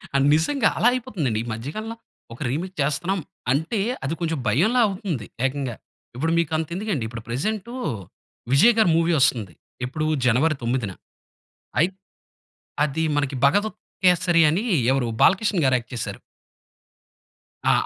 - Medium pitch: Yes, medium, 160 Hz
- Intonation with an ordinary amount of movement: No, wide, 6.3 semitones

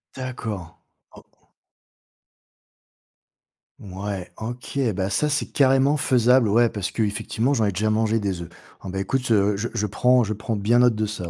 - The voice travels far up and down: No, average, 3.7 semitones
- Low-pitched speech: Yes, low, 110 Hz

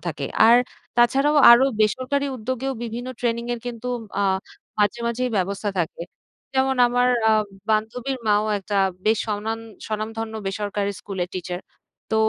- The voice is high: Yes, high, 225 Hz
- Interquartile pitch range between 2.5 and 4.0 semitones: Yes, average, 3.0 semitones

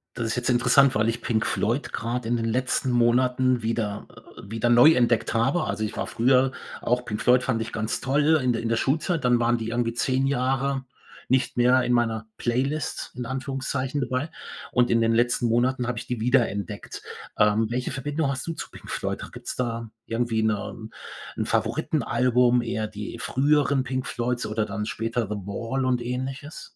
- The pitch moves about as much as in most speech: No, narrow, 2.2 semitones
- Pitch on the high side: No, low, 120 Hz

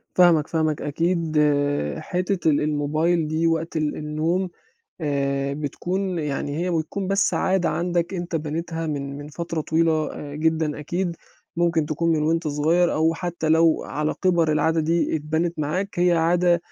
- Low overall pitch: No, medium, 160 Hz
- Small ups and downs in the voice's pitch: Yes, narrow, 2.2 semitones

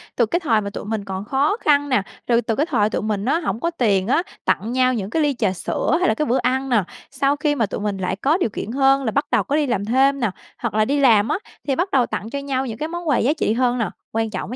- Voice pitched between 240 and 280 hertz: Yes, very high, 250 Hz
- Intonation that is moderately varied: Yes, average, 4.8 semitones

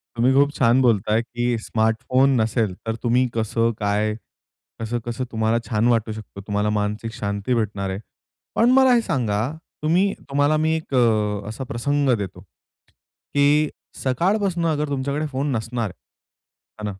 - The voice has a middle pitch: No, low, 115 Hz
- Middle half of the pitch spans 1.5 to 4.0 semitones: No, average, 4.6 semitones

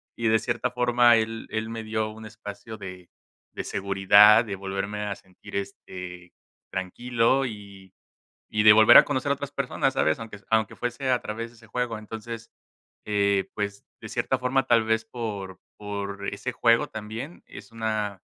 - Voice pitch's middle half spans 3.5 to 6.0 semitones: No, average, 2.8 semitones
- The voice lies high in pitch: No, low, 110 Hz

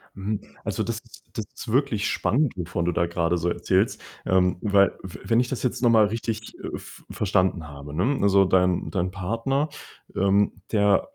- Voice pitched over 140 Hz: No, low, 100 Hz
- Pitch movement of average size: Yes, average, 4.2 semitones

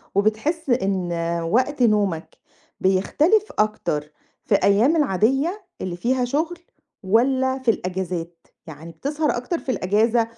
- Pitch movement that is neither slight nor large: No, wide, 6.4 semitones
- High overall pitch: Yes, high, 225 Hz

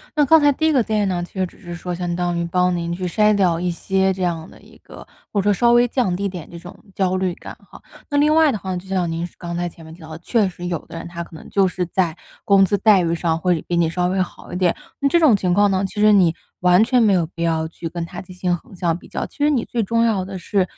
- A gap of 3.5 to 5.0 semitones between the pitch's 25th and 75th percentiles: No, average, 3.1 semitones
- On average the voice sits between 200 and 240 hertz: No, medium, 185 Hz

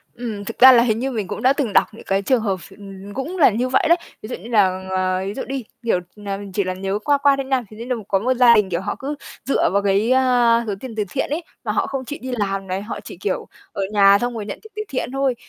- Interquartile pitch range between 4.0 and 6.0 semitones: Yes, average, 4.7 semitones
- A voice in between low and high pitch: No, high, 230 Hz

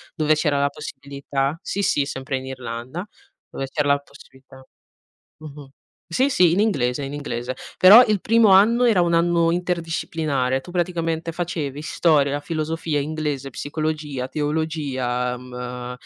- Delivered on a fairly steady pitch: No, average, 4.0 semitones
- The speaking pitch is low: No, medium, 150 Hz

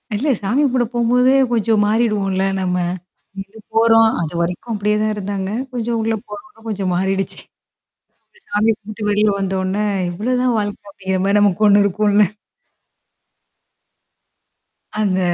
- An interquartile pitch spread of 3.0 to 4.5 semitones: No, narrow, 2.6 semitones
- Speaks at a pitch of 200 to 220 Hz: Yes, high, 210 Hz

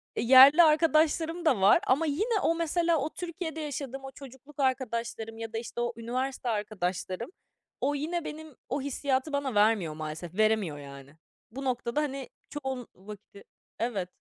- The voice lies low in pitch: No, very high, 260 Hz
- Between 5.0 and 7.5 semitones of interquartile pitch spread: Yes, average, 5.3 semitones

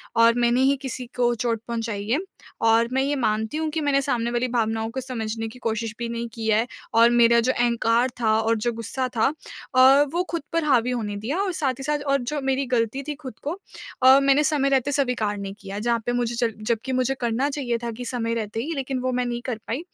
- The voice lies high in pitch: Yes, high, 240 Hz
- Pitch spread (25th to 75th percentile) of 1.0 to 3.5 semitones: Yes, average, 2.9 semitones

